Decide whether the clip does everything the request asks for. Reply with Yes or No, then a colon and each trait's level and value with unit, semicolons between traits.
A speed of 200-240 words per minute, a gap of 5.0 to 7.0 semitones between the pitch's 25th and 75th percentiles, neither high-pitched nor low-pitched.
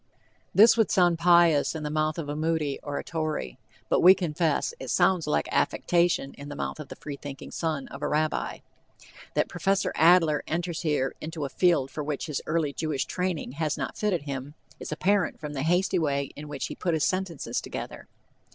No: fast, 205 wpm; average, 3.2 semitones; medium, 155 Hz